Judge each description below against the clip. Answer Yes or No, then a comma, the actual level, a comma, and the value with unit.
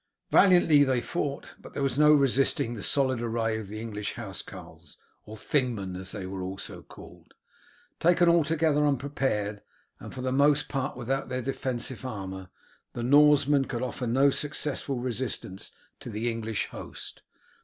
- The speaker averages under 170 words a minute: Yes, average, 155 wpm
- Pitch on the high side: No, low, 130 Hz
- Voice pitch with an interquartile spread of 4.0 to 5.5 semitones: Yes, average, 4.4 semitones